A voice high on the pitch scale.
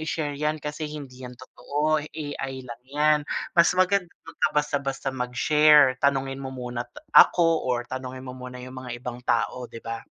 No: low, 135 Hz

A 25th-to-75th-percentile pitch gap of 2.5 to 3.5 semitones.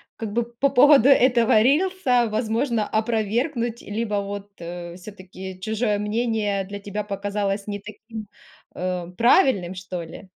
Yes: average, 3.1 semitones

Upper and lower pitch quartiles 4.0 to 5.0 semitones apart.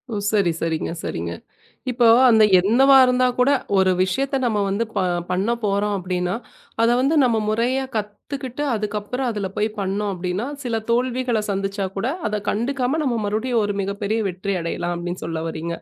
Yes: average, 4.5 semitones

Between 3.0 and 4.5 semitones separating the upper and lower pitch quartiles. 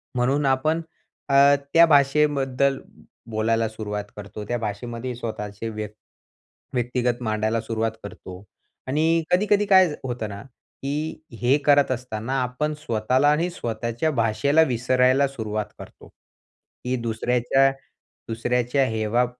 Yes: average, 3.9 semitones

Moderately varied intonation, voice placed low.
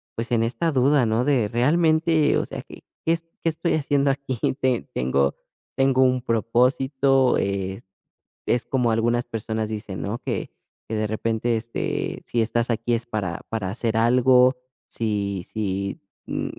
Yes: average, 3.2 semitones; low, 120 Hz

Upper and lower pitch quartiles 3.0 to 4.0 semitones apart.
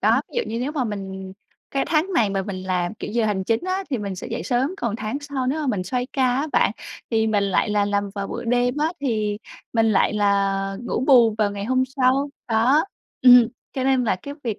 No: average, 4.5 semitones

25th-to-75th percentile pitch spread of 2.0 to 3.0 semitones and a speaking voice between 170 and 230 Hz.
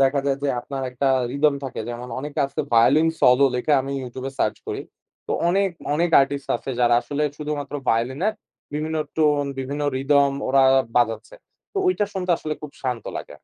No: average, 2.7 semitones; medium, 140 Hz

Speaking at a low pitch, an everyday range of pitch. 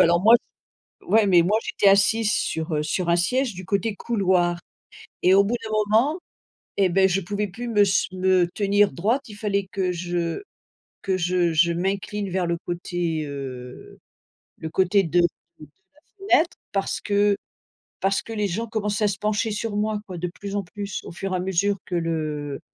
No: high, 190 Hz; average, 3.0 semitones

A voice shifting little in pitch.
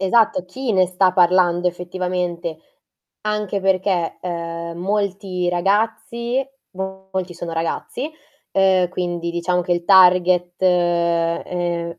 Yes: narrow, 1.8 semitones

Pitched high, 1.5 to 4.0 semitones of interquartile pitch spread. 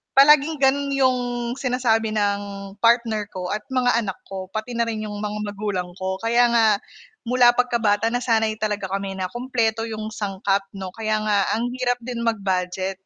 Yes: high, 220 Hz; average, 3.2 semitones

